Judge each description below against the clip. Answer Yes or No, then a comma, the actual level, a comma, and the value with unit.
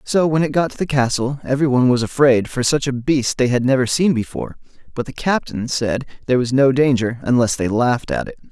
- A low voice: Yes, low, 130 Hz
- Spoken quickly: Yes, fast, 230 wpm